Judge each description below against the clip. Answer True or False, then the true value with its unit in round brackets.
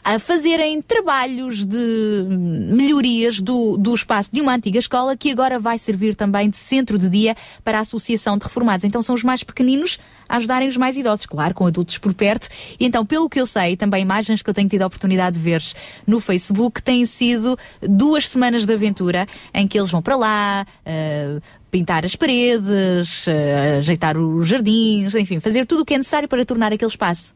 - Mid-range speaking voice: False (220 Hz)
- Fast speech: True (195 wpm)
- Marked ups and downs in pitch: False (4.6 semitones)